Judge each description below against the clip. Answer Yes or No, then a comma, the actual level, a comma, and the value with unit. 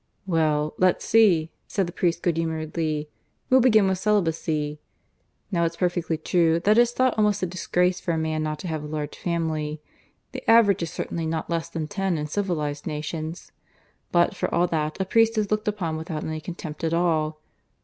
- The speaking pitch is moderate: Yes, medium, 165 Hz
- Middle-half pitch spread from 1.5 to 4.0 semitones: Yes, average, 3.3 semitones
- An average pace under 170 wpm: No, average, 190 wpm